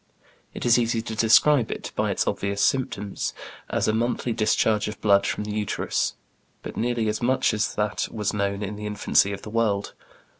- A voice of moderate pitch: No, low, 110 Hz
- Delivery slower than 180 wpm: No, average, 190 wpm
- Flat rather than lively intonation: Yes, narrow, 2.0 semitones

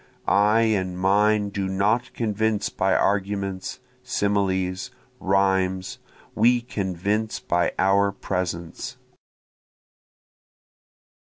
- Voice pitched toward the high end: No, low, 100 Hz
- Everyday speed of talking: No, slow, 80 wpm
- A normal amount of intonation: No, narrow, 2.2 semitones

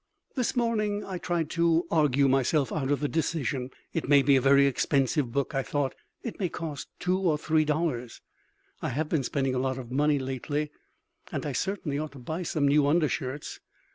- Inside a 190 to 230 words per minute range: Yes, average, 195 wpm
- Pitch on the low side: No, medium, 145 Hz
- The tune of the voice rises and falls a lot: No, average, 3.3 semitones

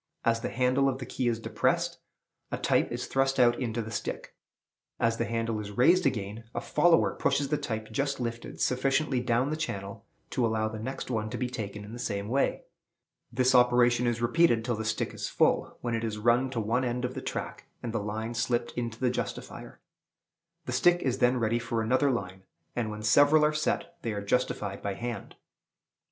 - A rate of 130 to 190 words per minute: No, fast, 205 wpm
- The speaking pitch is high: No, low, 120 Hz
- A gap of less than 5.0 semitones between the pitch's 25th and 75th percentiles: Yes, narrow, 2.6 semitones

